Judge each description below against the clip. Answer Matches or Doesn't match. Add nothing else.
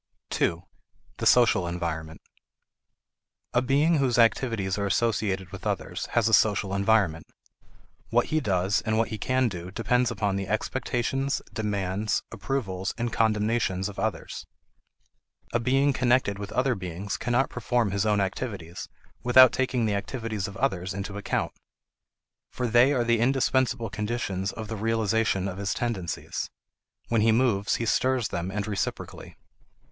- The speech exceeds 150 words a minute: Doesn't match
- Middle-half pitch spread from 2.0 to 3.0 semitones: Doesn't match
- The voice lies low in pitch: Matches